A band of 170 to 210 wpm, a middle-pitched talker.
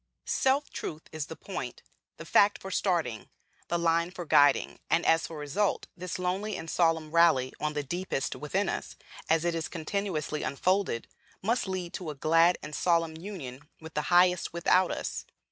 Yes: average, 175 wpm; medium, 170 Hz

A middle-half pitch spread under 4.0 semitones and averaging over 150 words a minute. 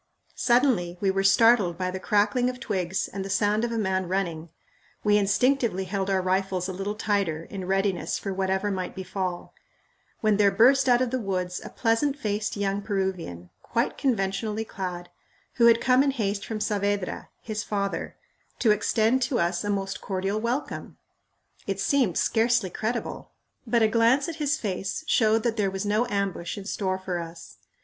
Yes: average, 3.3 semitones; average, 175 wpm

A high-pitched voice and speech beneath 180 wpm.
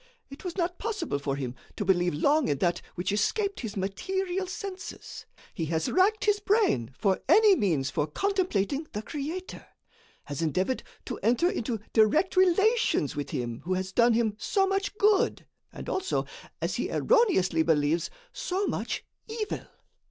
Yes: very high, 250 Hz; average, 160 wpm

